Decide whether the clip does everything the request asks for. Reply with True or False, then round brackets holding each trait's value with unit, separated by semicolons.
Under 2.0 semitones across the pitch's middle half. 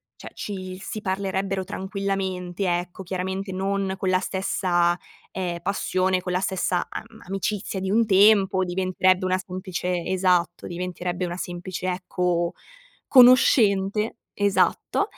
True (1.4 semitones)